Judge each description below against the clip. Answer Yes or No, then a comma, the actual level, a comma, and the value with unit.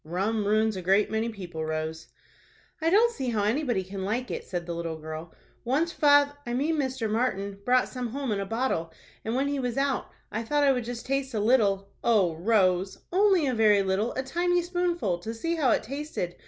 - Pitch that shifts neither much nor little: No, wide, 6.1 semitones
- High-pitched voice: Yes, high, 230 Hz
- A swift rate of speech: Yes, fast, 210 wpm